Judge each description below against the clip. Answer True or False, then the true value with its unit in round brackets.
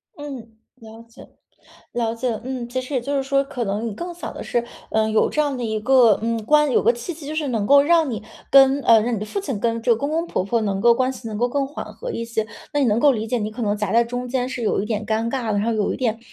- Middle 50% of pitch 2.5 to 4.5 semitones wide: True (3.5 semitones)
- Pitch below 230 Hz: False (240 Hz)